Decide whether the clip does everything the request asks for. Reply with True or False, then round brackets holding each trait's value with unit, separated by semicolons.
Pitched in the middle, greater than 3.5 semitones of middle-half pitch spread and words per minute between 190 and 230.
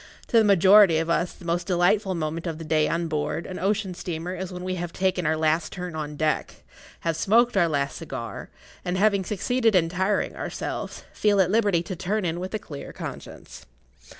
False (180 Hz; 3.1 semitones; 205 wpm)